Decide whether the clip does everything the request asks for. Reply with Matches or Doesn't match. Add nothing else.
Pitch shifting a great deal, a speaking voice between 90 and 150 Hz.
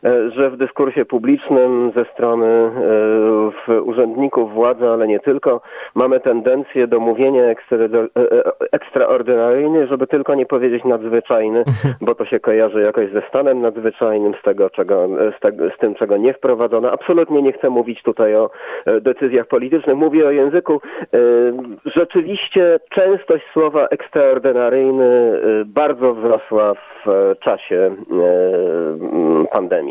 Matches